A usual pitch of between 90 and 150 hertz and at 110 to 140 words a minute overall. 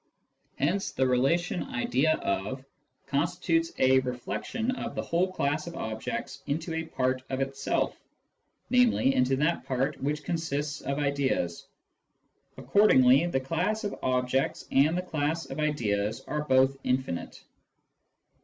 Yes: medium, 140 Hz; slow, 135 wpm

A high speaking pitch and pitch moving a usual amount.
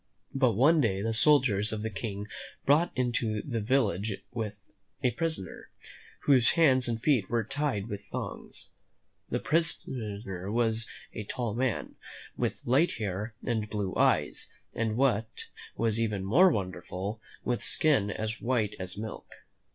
No: low, 115 Hz; average, 3.9 semitones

